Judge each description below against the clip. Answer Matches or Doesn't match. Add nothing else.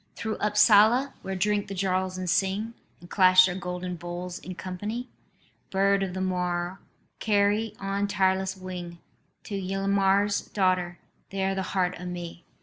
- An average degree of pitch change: Doesn't match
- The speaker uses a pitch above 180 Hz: Matches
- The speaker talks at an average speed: Matches